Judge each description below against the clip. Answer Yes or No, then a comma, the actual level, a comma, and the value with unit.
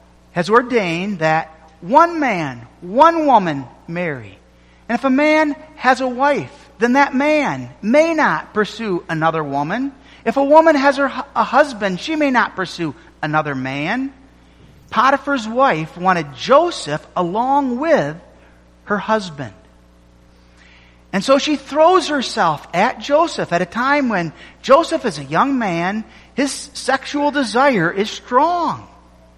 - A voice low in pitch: No, high, 220 Hz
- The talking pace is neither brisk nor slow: No, slow, 130 wpm